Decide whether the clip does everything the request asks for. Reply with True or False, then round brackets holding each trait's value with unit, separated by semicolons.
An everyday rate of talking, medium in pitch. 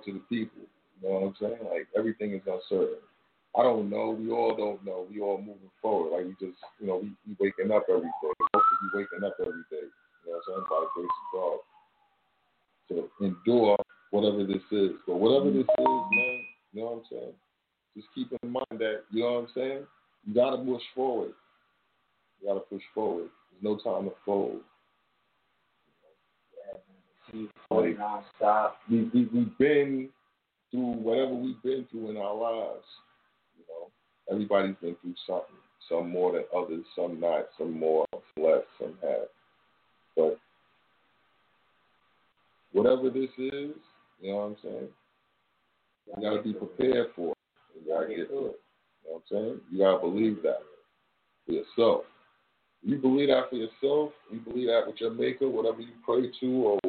False (175 wpm; 120 Hz)